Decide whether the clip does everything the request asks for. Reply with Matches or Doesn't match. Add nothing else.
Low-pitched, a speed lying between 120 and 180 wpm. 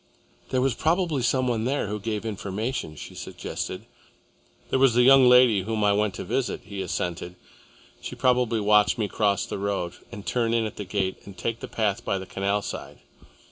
Doesn't match